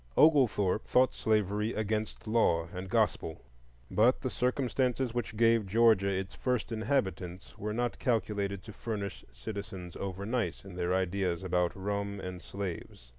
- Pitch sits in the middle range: No, low, 105 Hz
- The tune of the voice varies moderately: Yes, average, 3.5 semitones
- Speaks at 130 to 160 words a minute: Yes, average, 140 wpm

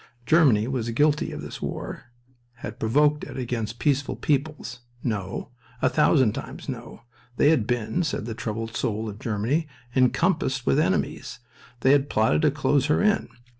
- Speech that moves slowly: No, average, 160 wpm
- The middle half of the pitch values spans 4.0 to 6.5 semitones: Yes, average, 4.7 semitones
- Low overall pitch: Yes, low, 130 Hz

